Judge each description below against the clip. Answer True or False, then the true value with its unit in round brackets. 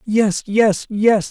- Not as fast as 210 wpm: True (140 wpm)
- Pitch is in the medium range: False (210 Hz)